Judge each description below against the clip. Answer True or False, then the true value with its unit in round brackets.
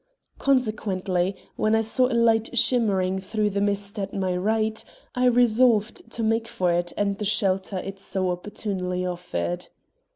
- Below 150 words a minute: False (155 wpm)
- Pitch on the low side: False (205 Hz)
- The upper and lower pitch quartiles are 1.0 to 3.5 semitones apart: True (3.1 semitones)